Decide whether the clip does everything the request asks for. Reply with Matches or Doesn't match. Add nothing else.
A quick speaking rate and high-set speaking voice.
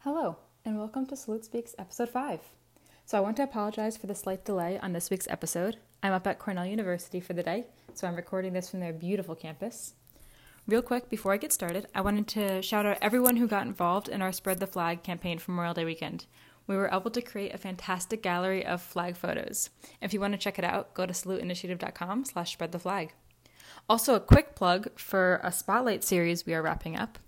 Matches